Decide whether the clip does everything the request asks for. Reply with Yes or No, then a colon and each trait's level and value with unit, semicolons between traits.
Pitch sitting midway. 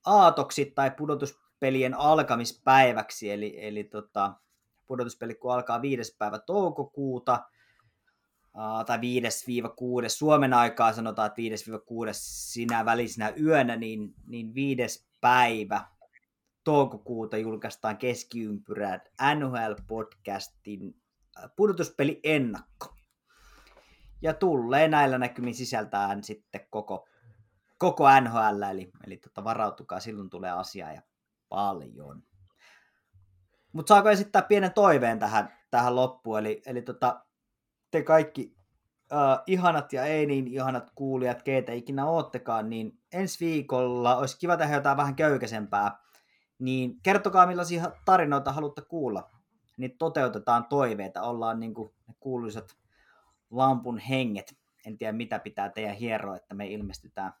No: low, 125 Hz